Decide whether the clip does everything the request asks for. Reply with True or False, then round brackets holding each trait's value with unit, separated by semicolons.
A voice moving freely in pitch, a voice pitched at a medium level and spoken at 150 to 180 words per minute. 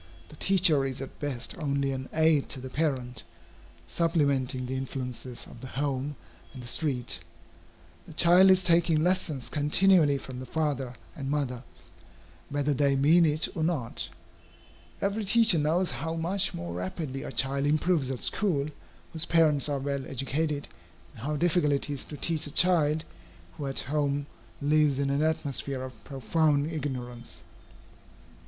False (3.3 semitones; 145 Hz; 155 wpm)